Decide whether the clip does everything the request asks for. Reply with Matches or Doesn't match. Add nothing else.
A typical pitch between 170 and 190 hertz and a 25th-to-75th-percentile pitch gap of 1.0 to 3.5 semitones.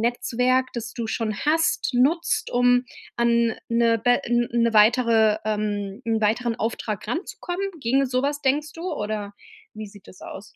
Doesn't match